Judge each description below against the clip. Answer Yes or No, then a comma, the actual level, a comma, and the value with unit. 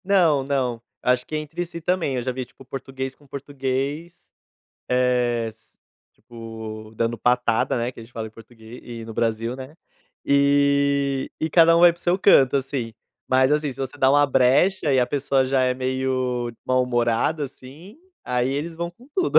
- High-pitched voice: No, low, 130 Hz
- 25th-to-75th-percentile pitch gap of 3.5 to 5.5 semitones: No, average, 3.0 semitones